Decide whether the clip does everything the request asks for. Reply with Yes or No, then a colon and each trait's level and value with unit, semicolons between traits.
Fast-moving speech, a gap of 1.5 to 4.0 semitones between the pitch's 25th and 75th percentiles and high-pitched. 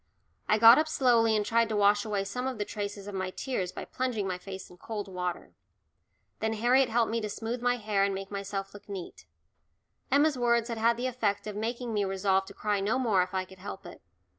Yes: fast, 230 wpm; average, 3.2 semitones; high, 210 Hz